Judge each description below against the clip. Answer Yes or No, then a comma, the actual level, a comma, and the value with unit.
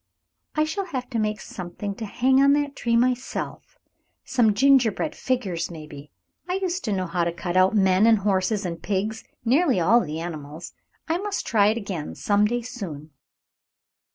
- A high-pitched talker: Yes, high, 215 Hz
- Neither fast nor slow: Yes, average, 175 wpm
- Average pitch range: No, wide, 5.9 semitones